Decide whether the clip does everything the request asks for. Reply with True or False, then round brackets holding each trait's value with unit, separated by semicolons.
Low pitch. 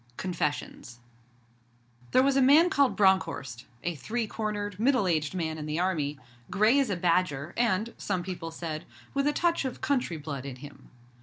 False (185 Hz)